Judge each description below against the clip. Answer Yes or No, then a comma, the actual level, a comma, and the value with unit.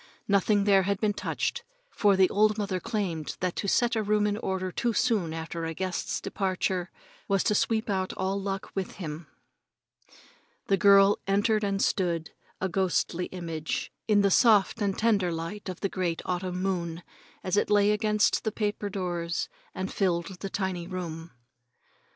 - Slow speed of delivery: No, average, 170 wpm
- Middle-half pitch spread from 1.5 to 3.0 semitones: Yes, narrow, 2.4 semitones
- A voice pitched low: No, high, 195 Hz